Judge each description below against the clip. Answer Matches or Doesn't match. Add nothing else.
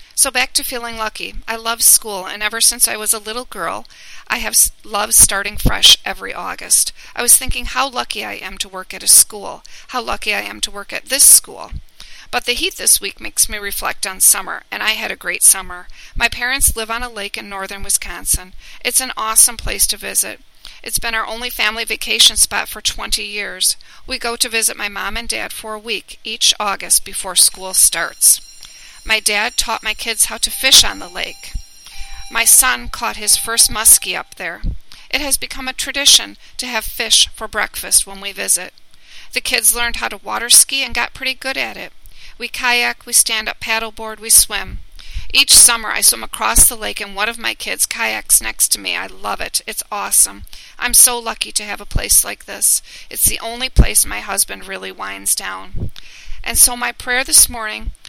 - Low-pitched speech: Doesn't match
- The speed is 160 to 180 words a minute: Doesn't match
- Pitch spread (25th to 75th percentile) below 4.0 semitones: Matches